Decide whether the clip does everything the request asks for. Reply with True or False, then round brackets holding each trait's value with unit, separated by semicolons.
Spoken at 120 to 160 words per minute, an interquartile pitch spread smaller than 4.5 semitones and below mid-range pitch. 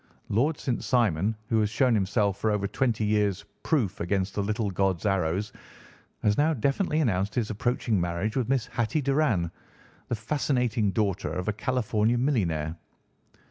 True (155 wpm; 4.0 semitones; 110 Hz)